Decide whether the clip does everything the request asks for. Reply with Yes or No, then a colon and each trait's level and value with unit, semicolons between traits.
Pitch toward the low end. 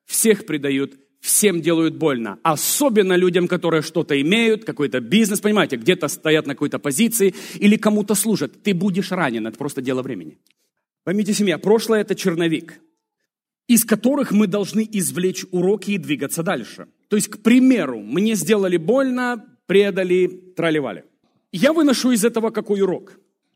No: high, 195 Hz